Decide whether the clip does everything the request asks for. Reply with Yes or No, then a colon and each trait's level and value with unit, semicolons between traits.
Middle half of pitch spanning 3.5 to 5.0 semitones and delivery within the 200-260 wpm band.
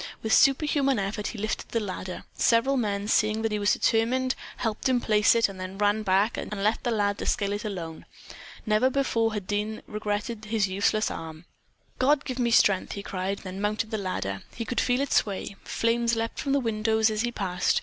No: narrow, 2.6 semitones; fast, 205 wpm